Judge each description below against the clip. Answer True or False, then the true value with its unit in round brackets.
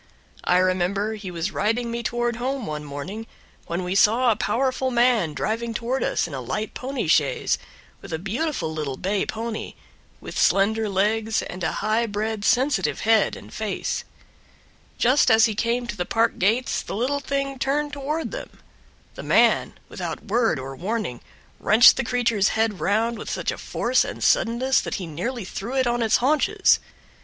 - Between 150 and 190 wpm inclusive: True (175 wpm)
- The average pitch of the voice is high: True (225 Hz)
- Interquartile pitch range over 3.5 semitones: True (4.0 semitones)